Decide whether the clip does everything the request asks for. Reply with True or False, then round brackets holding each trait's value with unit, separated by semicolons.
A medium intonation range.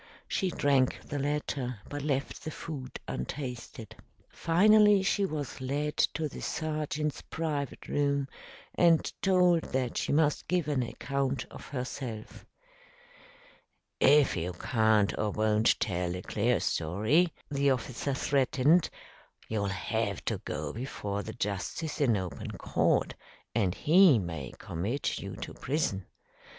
False (5.8 semitones)